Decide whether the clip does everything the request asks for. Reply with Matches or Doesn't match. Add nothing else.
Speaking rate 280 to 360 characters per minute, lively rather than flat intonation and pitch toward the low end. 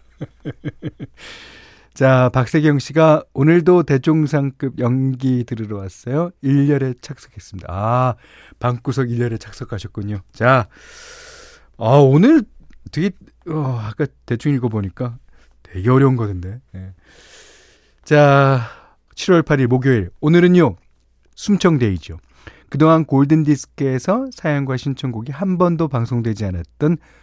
Doesn't match